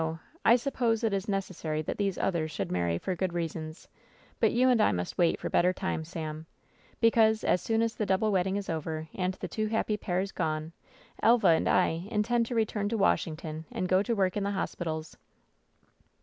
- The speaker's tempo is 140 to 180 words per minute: No, average, 195 wpm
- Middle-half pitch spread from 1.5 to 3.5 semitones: No, average, 5.0 semitones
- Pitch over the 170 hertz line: Yes, high, 190 Hz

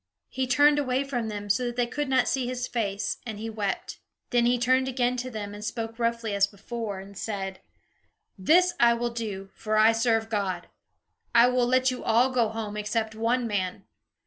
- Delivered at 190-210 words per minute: Yes, average, 200 wpm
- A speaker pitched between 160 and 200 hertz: No, high, 230 Hz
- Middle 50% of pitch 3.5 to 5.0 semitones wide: No, average, 3.0 semitones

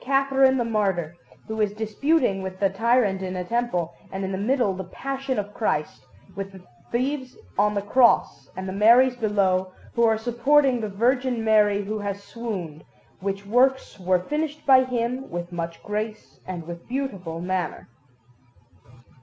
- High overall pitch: Yes, high, 210 Hz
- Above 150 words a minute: Yes, average, 160 wpm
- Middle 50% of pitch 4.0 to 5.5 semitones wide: Yes, average, 4.8 semitones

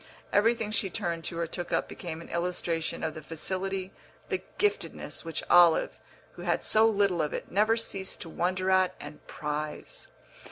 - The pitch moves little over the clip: No, average, 3.1 semitones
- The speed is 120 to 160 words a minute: No, average, 170 wpm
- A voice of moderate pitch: Yes, medium, 180 Hz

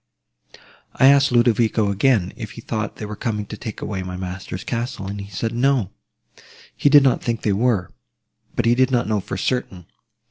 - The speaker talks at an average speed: Yes, average, 190 wpm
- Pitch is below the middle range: Yes, low, 110 Hz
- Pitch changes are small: No, average, 3.7 semitones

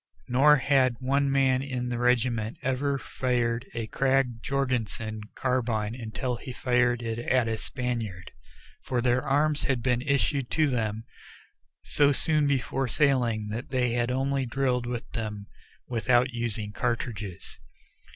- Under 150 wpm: Yes, average, 140 wpm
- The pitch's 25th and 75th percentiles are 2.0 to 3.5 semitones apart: Yes, narrow, 2.5 semitones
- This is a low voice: Yes, low, 125 Hz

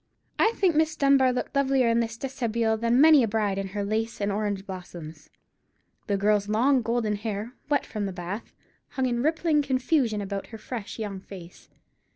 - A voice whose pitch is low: No, high, 225 Hz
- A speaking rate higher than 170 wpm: Yes, average, 185 wpm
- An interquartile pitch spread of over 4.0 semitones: Yes, average, 4.5 semitones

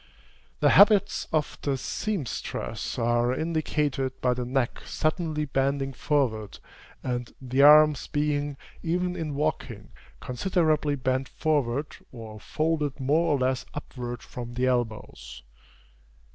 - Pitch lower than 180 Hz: Yes, medium, 140 Hz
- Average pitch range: Yes, average, 3.6 semitones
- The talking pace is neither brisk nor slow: No, slow, 115 wpm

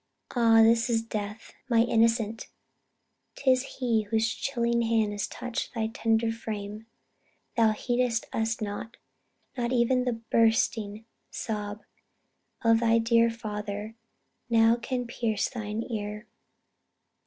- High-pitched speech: Yes, high, 225 Hz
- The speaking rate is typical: No, slow, 120 wpm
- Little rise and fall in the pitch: Yes, narrow, 1.3 semitones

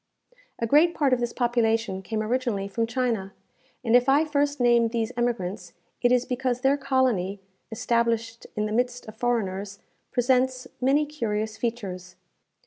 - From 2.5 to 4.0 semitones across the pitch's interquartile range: Yes, average, 2.8 semitones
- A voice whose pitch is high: Yes, high, 235 Hz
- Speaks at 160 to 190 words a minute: No, average, 150 wpm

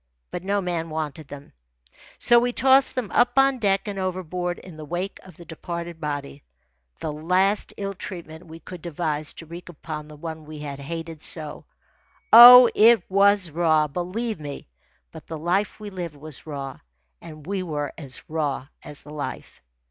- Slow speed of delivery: No, average, 175 wpm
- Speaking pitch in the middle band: Yes, medium, 170 Hz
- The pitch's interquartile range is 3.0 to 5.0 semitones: Yes, average, 4.2 semitones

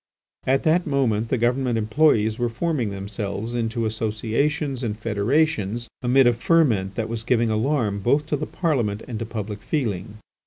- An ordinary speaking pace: Yes, average, 160 wpm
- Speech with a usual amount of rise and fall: Yes, average, 4.1 semitones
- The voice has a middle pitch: No, low, 115 Hz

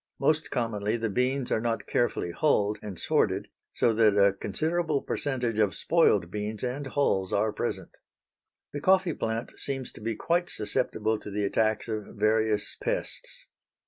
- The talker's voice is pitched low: Yes, low, 110 Hz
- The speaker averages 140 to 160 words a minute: Yes, average, 155 wpm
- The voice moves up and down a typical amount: Yes, average, 4.2 semitones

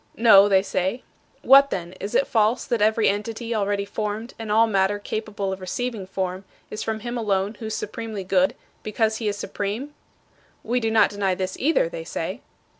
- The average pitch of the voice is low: No, high, 215 Hz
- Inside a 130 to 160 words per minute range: No, average, 190 wpm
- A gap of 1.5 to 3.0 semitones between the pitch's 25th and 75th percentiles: Yes, narrow, 2.5 semitones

